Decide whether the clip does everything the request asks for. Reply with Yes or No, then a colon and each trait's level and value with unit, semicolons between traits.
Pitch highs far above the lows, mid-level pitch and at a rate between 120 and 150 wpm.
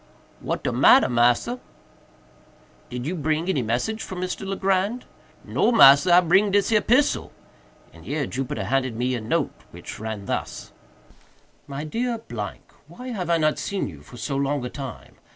No: wide, 7.6 semitones; medium, 155 Hz; average, 165 wpm